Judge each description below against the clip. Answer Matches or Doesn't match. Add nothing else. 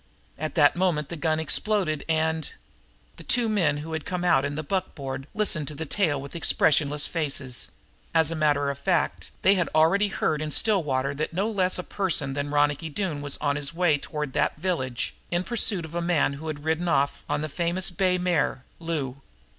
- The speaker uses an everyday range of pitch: Matches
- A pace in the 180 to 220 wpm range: Matches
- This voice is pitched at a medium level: Matches